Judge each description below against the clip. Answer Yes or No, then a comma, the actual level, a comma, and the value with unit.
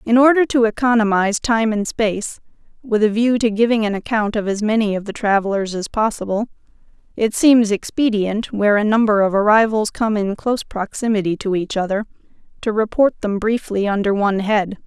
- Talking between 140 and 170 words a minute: No, average, 180 wpm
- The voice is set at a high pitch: Yes, high, 215 Hz